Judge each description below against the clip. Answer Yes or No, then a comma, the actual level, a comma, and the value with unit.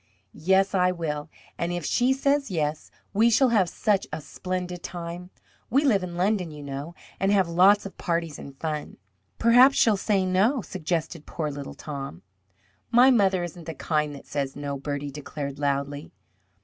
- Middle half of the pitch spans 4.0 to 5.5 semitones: Yes, average, 4.9 semitones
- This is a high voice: No, medium, 175 Hz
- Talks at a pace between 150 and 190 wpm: Yes, average, 175 wpm